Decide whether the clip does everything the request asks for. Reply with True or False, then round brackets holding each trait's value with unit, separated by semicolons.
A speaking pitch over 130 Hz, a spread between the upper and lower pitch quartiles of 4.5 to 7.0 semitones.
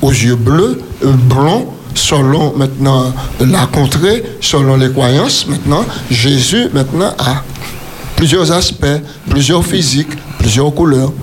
False (140 Hz; 2.4 semitones)